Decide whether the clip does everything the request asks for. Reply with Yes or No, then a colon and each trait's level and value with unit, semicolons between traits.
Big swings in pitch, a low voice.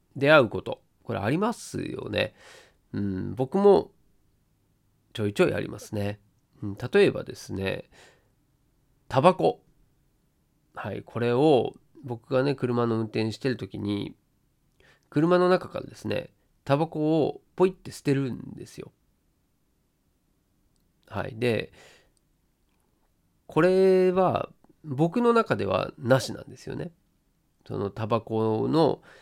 Yes: wide, 7.4 semitones; low, 125 Hz